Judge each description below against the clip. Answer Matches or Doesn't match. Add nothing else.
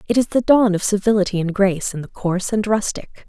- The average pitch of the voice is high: Matches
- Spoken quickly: Matches